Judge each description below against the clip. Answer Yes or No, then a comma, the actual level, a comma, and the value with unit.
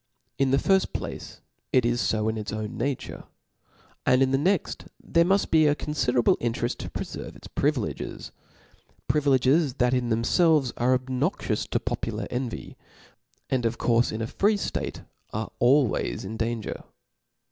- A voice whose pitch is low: Yes, low, 125 Hz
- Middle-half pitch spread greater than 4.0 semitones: No, average, 3.7 semitones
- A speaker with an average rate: Yes, average, 160 wpm